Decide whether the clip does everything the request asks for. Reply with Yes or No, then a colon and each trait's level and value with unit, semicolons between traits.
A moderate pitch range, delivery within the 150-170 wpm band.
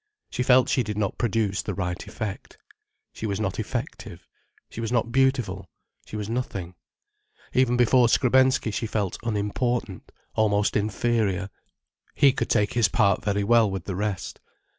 Yes: average, 3.3 semitones; average, 155 wpm